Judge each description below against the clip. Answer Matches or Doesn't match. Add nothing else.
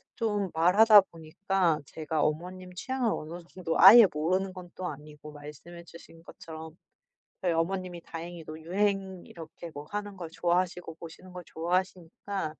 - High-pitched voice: Doesn't match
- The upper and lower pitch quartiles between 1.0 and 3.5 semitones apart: Matches